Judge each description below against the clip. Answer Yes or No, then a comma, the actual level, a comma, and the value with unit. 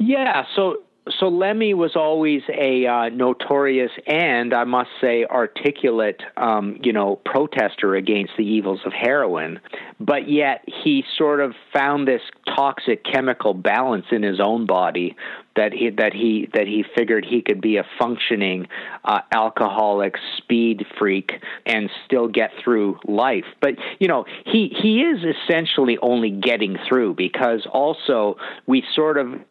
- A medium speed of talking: Yes, average, 150 wpm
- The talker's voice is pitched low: Yes, low, 120 Hz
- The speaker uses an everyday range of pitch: No, wide, 5.7 semitones